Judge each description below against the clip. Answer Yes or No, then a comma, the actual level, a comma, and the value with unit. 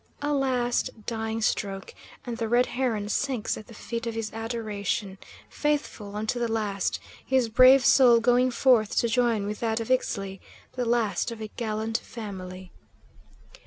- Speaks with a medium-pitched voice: No, high, 225 Hz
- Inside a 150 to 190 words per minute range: Yes, average, 160 wpm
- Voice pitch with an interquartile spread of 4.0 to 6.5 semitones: No, narrow, 2.6 semitones